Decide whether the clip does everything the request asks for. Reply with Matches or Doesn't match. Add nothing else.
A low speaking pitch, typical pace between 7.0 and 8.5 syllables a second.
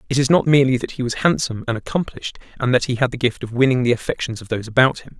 Matches